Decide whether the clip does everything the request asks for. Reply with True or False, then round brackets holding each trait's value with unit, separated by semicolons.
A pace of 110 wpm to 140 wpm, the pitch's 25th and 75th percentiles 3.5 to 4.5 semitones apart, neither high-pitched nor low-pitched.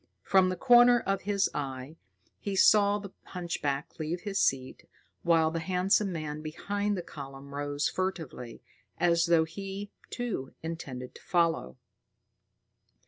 False (135 wpm; 5.0 semitones; 170 Hz)